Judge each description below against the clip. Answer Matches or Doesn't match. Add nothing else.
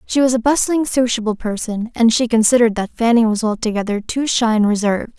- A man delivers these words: Doesn't match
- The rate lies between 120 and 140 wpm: Doesn't match